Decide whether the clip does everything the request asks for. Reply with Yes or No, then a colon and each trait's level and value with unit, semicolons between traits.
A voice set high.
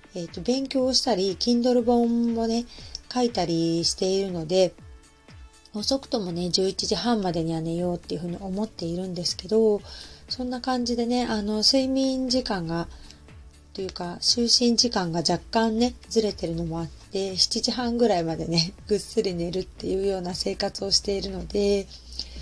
Yes: high, 195 Hz